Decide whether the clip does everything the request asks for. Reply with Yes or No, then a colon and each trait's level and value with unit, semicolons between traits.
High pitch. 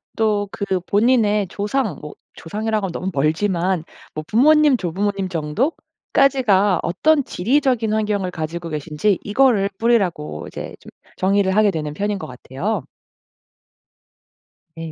Yes: high, 200 Hz